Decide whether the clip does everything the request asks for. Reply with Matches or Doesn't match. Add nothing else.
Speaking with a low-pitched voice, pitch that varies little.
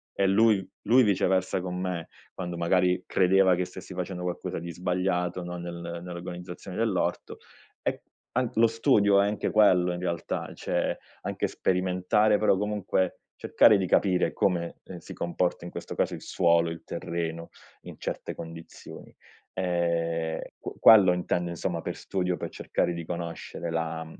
Matches